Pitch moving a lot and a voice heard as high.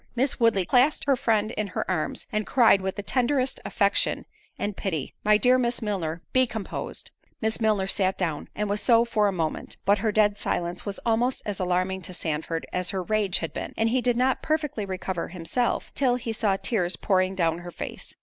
No: average, 4.2 semitones; high, 205 Hz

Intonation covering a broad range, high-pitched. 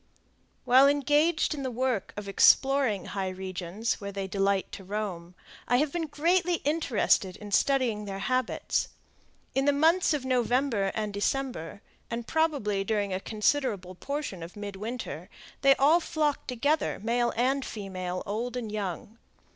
Yes: wide, 5.8 semitones; high, 230 Hz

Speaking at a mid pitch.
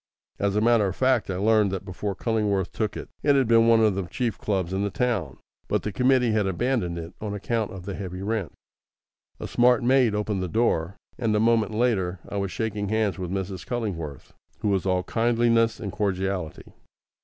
No: low, 105 Hz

